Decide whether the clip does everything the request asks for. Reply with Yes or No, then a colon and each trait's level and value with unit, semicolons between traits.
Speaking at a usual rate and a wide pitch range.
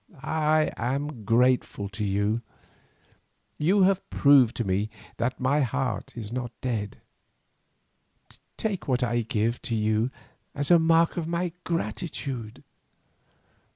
No: slow, 120 wpm; wide, 5.7 semitones